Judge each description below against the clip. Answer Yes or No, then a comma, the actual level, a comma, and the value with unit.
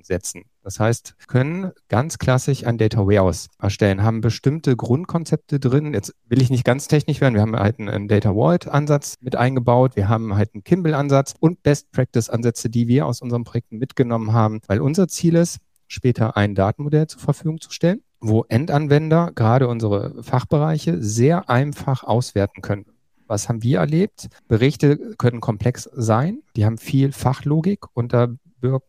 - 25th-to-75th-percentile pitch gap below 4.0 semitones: No, average, 4.7 semitones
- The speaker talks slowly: No, average, 165 wpm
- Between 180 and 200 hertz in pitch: No, low, 125 Hz